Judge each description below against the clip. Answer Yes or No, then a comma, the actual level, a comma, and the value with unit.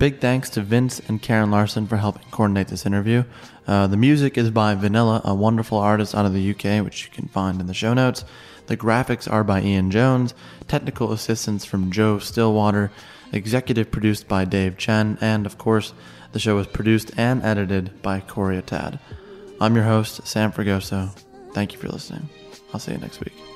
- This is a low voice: Yes, low, 110 Hz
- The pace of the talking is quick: No, average, 190 wpm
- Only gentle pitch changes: Yes, narrow, 2.3 semitones